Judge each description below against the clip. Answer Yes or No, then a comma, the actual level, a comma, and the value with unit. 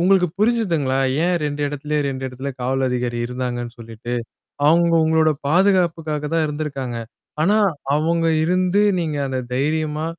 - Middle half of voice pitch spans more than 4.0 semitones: Yes, average, 4.4 semitones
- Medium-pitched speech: Yes, medium, 150 Hz